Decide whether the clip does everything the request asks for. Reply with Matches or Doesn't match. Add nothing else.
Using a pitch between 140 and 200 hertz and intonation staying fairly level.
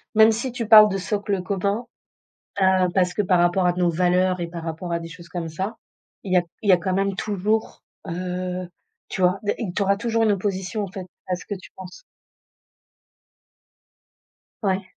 Matches